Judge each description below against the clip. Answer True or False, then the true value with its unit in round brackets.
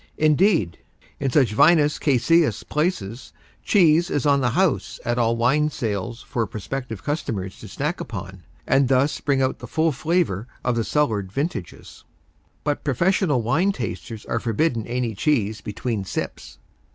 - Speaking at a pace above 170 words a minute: False (150 wpm)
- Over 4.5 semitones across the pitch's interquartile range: True (5.2 semitones)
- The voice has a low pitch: True (130 Hz)